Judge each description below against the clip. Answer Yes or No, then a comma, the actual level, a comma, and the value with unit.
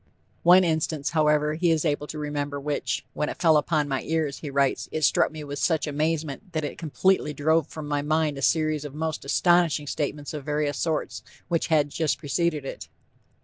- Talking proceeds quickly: No, average, 195 wpm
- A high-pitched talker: No, medium, 150 Hz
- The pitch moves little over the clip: Yes, narrow, 1.8 semitones